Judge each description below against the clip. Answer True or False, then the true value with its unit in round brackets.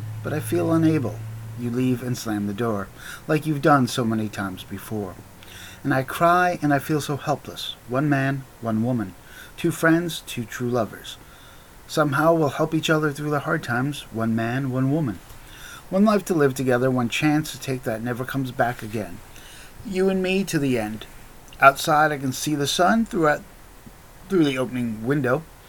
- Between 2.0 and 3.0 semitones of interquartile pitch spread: False (5.0 semitones)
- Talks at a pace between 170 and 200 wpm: True (180 wpm)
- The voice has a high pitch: False (135 Hz)